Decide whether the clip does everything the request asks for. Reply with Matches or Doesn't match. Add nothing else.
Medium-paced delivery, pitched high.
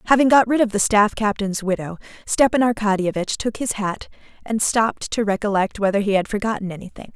Matches